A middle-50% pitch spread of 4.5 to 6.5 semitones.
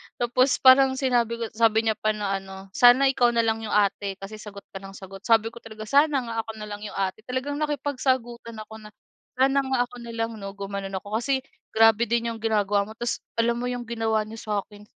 No: average, 2.8 semitones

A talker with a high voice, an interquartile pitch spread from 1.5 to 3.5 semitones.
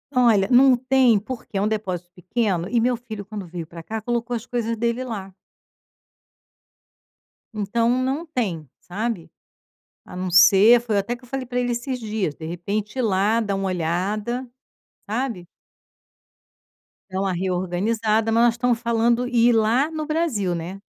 No: high, 220 Hz; average, 4.0 semitones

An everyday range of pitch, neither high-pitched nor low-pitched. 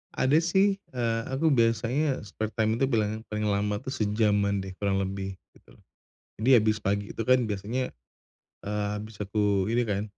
No: average, 3.0 semitones; low, 110 Hz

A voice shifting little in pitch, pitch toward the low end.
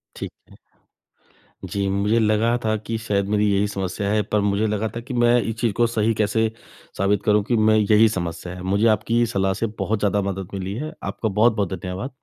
Yes: narrow, 2.3 semitones; low, 105 Hz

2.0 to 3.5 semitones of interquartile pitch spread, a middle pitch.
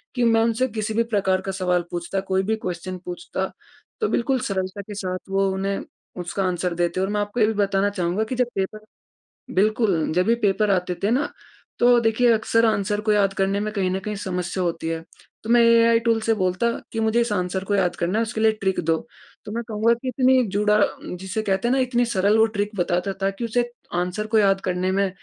No: average, 3.1 semitones; high, 205 Hz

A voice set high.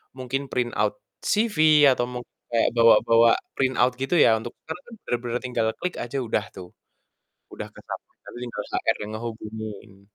No: low, 120 Hz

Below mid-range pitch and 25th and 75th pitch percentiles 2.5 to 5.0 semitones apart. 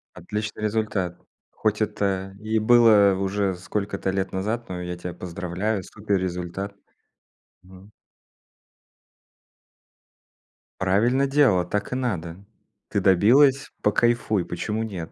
Yes: low, 100 Hz; average, 2.8 semitones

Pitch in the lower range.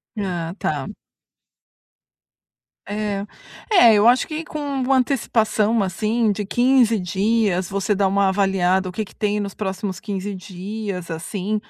No: high, 205 Hz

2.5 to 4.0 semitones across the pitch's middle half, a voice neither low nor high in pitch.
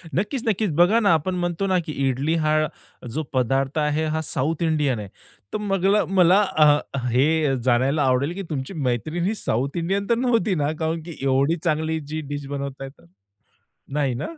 No: average, 4.5 semitones; medium, 155 Hz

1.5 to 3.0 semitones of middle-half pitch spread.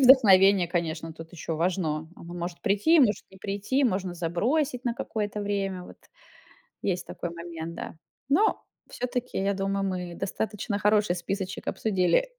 No: average, 3.4 semitones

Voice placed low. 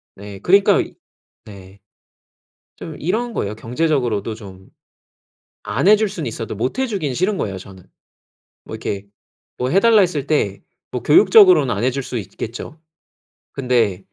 Yes: low, 125 Hz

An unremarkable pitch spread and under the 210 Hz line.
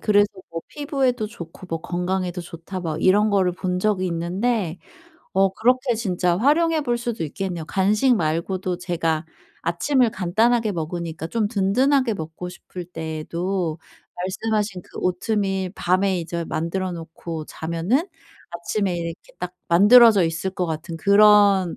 Yes: average, 3.9 semitones; medium, 185 Hz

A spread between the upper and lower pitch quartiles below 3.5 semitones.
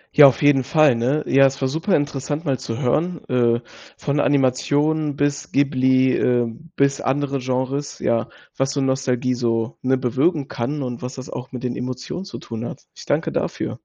Yes: narrow, 2.4 semitones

